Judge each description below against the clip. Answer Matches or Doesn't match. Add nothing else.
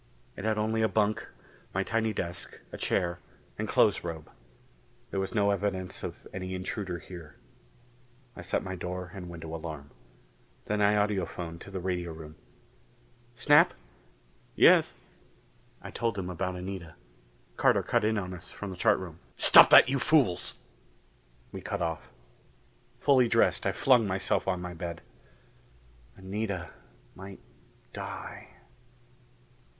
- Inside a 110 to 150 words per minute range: Matches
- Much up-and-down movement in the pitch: Doesn't match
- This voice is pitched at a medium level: Doesn't match